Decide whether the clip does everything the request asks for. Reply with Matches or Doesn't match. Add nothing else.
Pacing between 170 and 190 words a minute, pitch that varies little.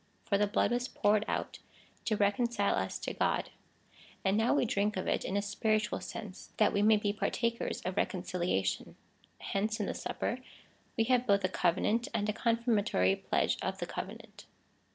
Matches